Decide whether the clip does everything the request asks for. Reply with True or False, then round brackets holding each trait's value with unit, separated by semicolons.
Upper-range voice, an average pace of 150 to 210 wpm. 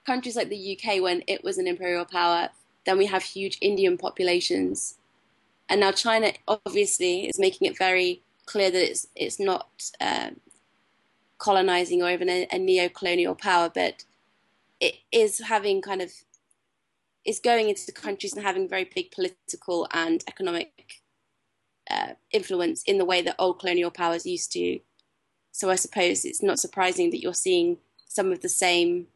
True (205 Hz; 165 wpm)